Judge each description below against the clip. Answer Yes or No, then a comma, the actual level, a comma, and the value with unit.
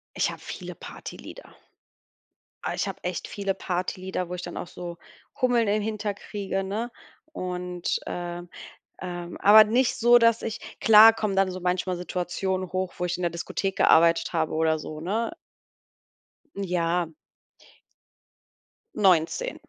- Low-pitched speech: No, medium, 185 Hz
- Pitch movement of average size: Yes, average, 3.3 semitones